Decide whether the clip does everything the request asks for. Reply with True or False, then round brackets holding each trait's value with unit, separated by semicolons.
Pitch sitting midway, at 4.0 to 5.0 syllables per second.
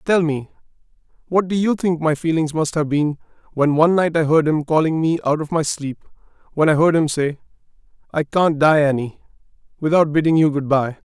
False (155 Hz; 5.4 syllables/s)